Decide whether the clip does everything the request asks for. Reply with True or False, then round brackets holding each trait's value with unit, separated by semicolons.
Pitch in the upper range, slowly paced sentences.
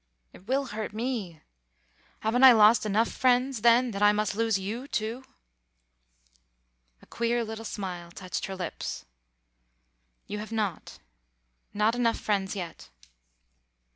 True (215 Hz; 130 wpm)